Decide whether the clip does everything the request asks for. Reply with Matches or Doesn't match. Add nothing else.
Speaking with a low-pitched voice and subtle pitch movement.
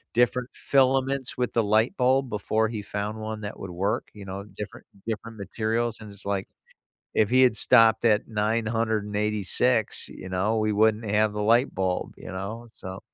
Matches